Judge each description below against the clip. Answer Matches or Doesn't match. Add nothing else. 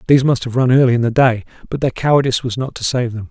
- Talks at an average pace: Doesn't match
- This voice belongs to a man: Matches